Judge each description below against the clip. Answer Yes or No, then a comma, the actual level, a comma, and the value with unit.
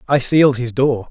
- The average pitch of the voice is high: No, low, 130 Hz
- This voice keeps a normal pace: No, fast, 215 wpm